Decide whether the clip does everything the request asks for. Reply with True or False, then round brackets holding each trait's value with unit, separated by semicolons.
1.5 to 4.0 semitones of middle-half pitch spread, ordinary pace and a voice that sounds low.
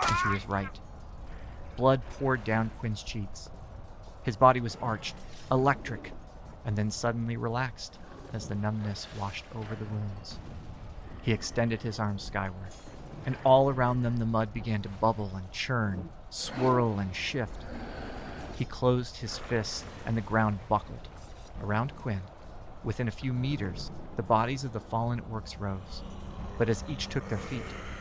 True (3.6 semitones; 150 wpm; 110 Hz)